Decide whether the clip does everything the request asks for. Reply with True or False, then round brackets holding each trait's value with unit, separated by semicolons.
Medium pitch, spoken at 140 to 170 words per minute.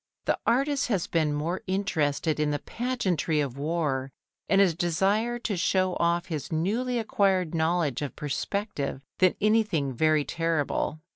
True (170 Hz; 145 wpm)